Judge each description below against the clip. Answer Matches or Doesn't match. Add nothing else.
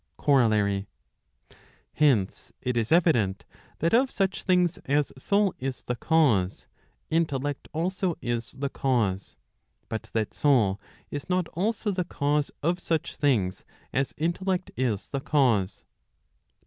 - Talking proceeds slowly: Matches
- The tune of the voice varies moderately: Doesn't match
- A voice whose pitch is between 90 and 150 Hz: Matches